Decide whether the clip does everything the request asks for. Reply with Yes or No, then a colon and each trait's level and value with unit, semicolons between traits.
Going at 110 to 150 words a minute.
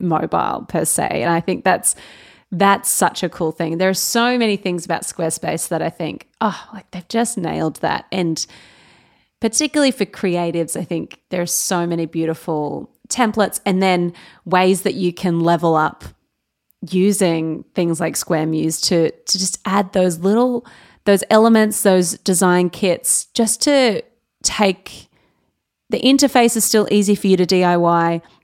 No: average, 160 wpm